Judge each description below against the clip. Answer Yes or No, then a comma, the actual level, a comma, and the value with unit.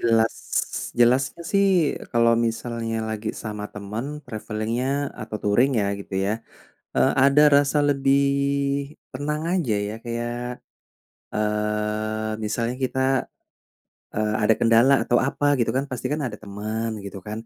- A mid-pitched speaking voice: No, low, 115 Hz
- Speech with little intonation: No, average, 3.1 semitones